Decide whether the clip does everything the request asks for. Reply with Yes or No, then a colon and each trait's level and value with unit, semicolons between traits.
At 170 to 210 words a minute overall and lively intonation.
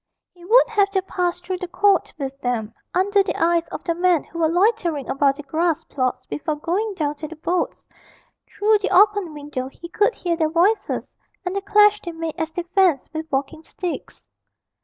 No: average, 200 wpm; average, 3.9 semitones